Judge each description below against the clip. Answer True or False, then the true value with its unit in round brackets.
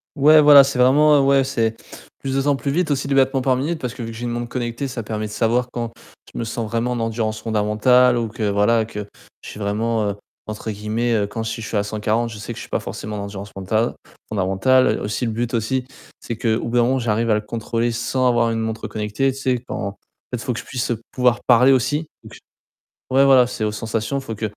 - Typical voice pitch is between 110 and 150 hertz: True (115 Hz)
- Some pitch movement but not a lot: True (3.0 semitones)